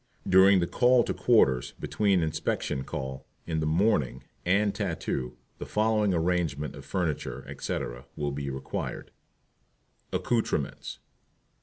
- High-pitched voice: No, very low, 85 Hz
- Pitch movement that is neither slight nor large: No, wide, 6.6 semitones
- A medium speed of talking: No, slow, 120 wpm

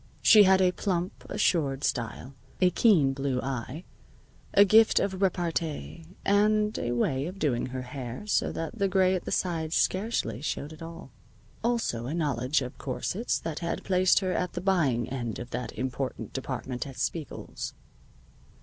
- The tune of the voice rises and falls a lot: Yes, wide, 6.3 semitones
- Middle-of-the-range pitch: Yes, medium, 160 Hz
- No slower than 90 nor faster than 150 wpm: No, average, 165 wpm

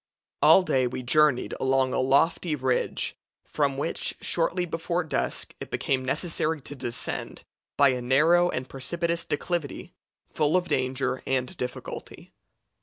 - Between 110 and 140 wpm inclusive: Yes, slow, 135 wpm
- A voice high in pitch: No, medium, 140 Hz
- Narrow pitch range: No, average, 4.3 semitones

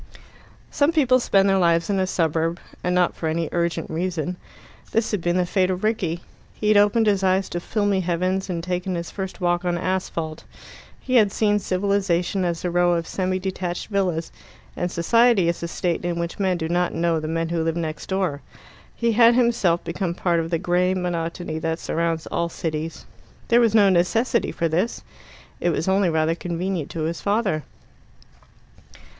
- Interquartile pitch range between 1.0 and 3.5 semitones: Yes, narrow, 2.6 semitones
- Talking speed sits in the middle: Yes, average, 185 wpm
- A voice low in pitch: No, medium, 180 Hz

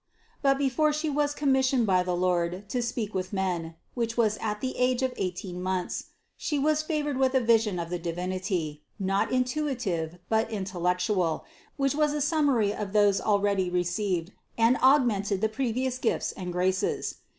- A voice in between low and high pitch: No, high, 210 Hz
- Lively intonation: Yes, wide, 6.1 semitones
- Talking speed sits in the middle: Yes, average, 165 wpm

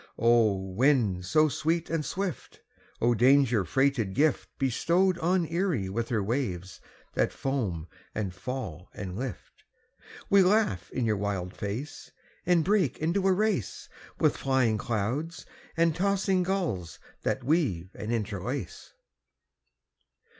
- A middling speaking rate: No, slow, 125 wpm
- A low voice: Yes, low, 130 Hz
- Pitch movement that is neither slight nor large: No, wide, 8.5 semitones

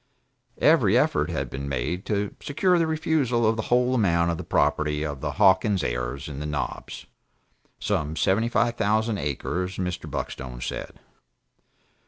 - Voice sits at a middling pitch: No, very low, 95 Hz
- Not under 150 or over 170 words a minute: Yes, average, 155 wpm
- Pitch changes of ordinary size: No, wide, 7.5 semitones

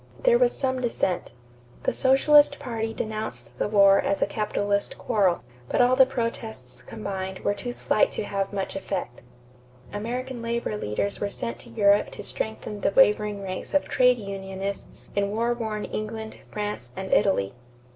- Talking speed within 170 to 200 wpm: No, average, 160 wpm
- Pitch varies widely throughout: No, average, 3.2 semitones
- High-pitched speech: Yes, high, 210 Hz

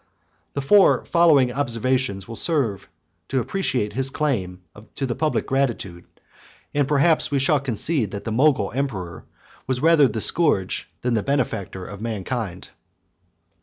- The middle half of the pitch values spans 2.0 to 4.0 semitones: No, wide, 5.4 semitones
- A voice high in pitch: No, low, 130 Hz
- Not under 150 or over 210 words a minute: No, average, 140 wpm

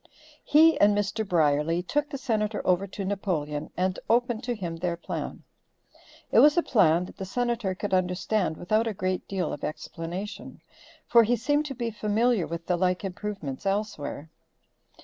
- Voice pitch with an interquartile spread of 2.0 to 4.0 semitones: No, average, 4.4 semitones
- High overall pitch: Yes, high, 195 Hz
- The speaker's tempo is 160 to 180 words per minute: Yes, average, 170 wpm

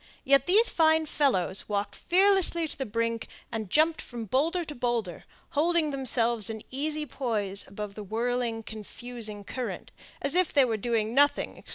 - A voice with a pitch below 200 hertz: No, high, 245 Hz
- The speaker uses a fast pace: No, average, 165 wpm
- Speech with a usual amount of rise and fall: No, wide, 5.7 semitones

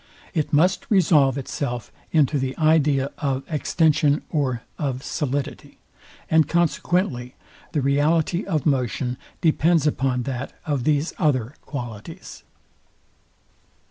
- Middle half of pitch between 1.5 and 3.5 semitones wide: Yes, average, 3.2 semitones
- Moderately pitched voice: Yes, medium, 145 Hz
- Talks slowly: Yes, slow, 110 wpm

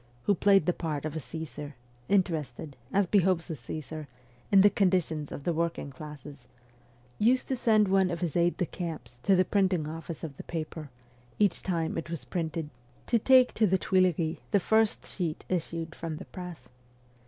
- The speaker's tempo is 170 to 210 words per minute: Yes, average, 180 wpm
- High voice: No, medium, 170 Hz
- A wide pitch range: No, average, 3.5 semitones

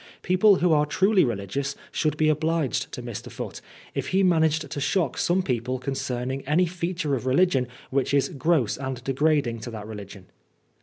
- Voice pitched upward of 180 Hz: No, medium, 145 Hz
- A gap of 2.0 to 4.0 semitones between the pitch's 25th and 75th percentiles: No, average, 4.8 semitones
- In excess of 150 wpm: Yes, average, 170 wpm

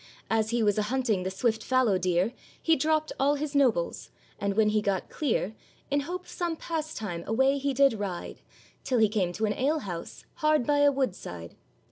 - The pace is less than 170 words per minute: No, average, 195 wpm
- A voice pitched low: No, high, 235 Hz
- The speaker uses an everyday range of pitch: No, wide, 6.0 semitones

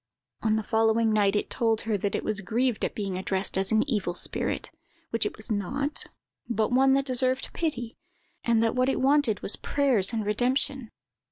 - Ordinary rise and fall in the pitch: Yes, average, 3.6 semitones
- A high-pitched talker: Yes, high, 225 Hz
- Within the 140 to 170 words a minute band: No, average, 190 wpm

